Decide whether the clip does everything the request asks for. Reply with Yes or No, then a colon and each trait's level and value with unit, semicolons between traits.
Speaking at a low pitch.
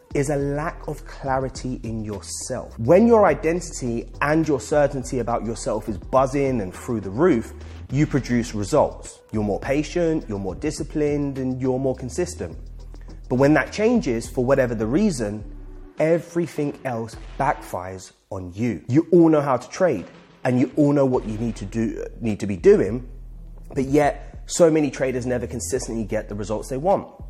Yes: low, 130 Hz